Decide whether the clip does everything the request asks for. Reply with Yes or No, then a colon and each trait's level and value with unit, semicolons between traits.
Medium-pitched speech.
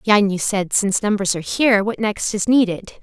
No: high, 205 Hz